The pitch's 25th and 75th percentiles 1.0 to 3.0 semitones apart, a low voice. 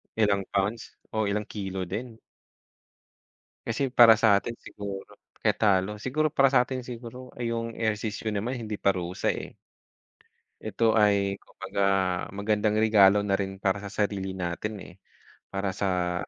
Yes: average, 2.7 semitones; low, 105 Hz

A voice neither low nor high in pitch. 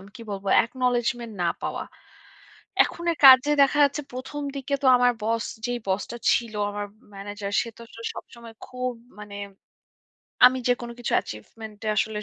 No: high, 240 Hz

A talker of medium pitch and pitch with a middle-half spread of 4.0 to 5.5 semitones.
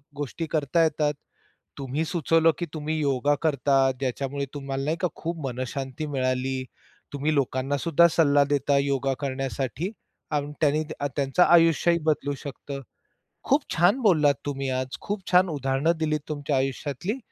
No: medium, 145 Hz; average, 2.9 semitones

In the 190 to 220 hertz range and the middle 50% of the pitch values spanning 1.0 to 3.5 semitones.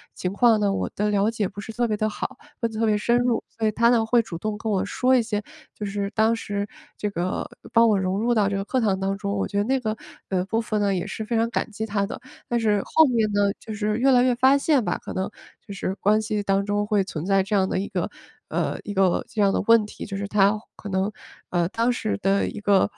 Yes: high, 210 Hz; narrow, 2.4 semitones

